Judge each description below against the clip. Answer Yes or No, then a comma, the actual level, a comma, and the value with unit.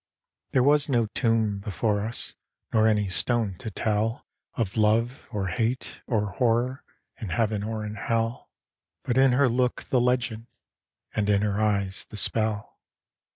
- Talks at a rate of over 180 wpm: No, average, 155 wpm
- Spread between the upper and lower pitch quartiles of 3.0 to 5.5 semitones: No, narrow, 2.5 semitones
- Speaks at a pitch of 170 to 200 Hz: No, low, 110 Hz